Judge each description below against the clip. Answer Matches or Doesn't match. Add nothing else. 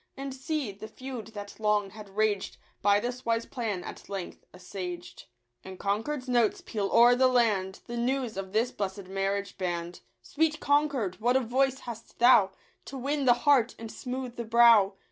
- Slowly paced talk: Doesn't match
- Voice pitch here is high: Matches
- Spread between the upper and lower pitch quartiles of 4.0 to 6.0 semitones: Matches